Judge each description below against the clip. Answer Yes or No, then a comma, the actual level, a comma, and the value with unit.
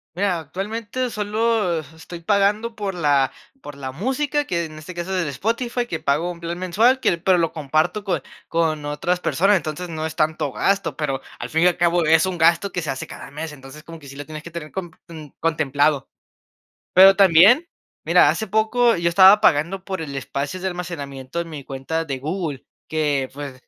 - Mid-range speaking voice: Yes, medium, 170 Hz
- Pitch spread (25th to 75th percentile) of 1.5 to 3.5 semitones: No, average, 4.3 semitones